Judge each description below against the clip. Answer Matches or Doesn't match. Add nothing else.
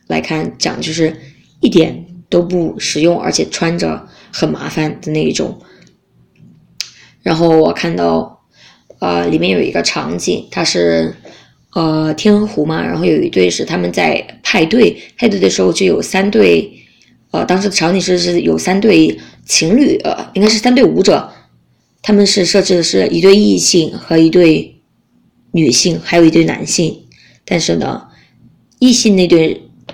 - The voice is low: Doesn't match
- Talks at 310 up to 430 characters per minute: Doesn't match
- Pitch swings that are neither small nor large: Matches